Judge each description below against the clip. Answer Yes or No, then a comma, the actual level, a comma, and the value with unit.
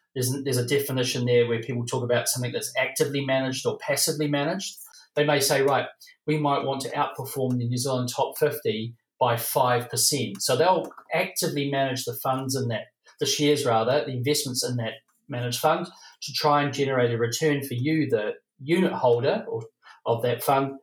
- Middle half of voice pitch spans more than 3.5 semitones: No, average, 3.2 semitones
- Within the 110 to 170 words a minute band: No, average, 185 wpm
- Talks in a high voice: No, low, 135 Hz